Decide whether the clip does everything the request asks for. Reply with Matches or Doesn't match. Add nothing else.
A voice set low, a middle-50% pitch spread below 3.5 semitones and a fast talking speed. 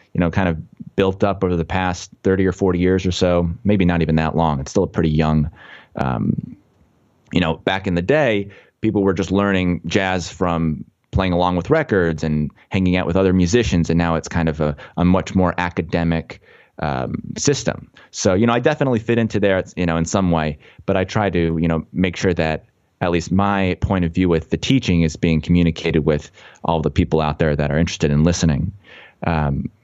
Matches